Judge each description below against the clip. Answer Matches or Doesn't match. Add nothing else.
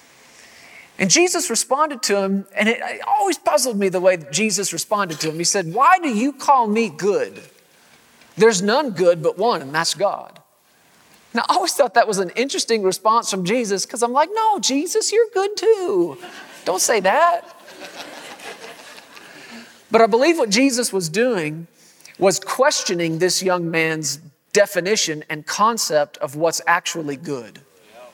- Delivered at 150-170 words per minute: Matches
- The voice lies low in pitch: Doesn't match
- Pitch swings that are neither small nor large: Doesn't match